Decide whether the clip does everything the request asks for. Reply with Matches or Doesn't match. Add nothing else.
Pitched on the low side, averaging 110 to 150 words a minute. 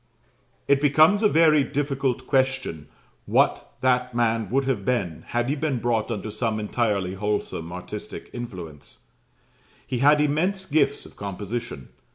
Matches